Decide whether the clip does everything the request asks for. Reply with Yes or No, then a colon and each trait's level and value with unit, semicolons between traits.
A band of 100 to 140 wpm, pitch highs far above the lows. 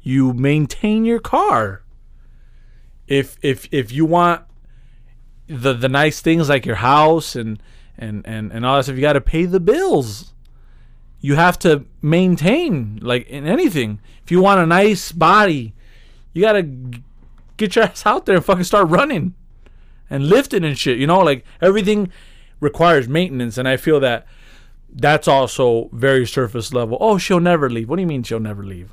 No: average, 170 wpm; wide, 6.1 semitones